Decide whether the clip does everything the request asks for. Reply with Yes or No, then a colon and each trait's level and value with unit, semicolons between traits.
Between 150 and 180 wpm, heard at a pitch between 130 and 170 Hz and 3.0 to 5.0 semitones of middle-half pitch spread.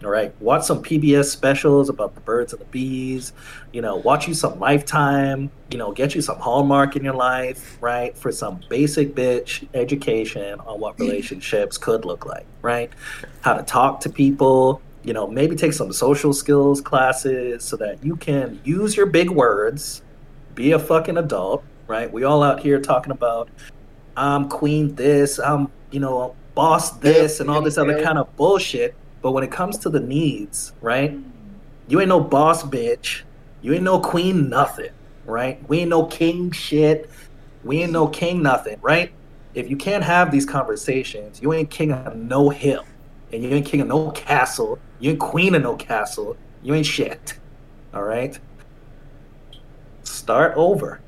No: average, 175 wpm; medium, 140 Hz; narrow, 2.6 semitones